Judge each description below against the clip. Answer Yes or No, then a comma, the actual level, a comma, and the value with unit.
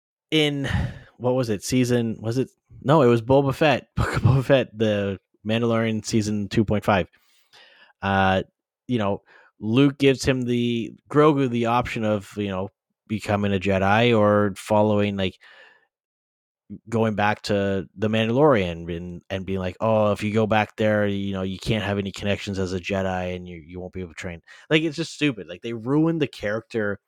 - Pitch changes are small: No, average, 3.7 semitones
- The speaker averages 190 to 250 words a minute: No, average, 175 wpm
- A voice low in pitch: Yes, low, 105 Hz